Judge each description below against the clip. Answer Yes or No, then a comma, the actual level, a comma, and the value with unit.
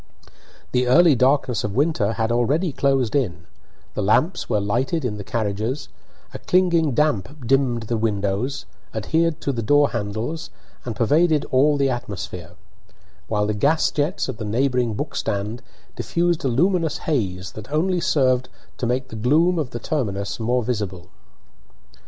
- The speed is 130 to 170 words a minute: Yes, average, 155 wpm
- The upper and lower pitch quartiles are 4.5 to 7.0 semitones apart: Yes, wide, 5.6 semitones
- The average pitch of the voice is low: Yes, low, 125 Hz